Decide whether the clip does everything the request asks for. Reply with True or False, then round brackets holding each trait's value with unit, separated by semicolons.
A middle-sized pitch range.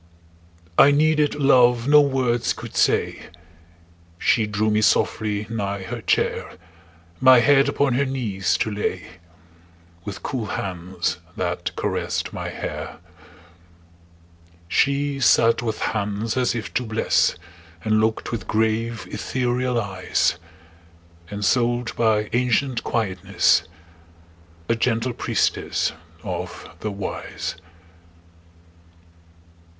True (3.4 semitones)